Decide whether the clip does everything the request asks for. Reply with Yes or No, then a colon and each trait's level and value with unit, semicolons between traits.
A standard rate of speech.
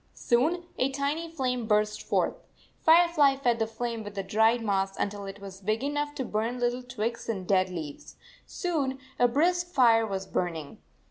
Yes: average, 175 wpm